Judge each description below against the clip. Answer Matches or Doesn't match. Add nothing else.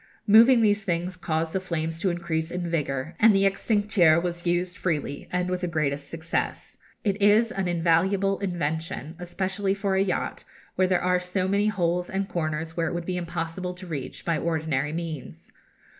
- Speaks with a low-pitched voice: Doesn't match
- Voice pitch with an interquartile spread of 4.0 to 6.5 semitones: Doesn't match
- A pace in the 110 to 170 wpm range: Doesn't match